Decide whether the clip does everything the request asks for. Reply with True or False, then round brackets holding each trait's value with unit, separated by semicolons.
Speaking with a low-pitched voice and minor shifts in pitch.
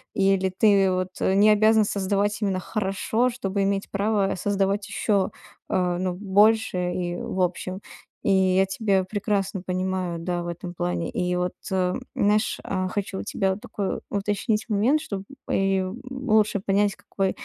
False (195 Hz; 1.8 semitones)